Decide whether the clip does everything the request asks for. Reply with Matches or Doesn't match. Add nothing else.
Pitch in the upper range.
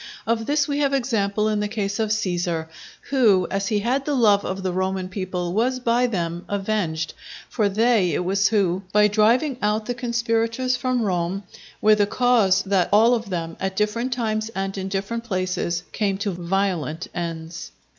Matches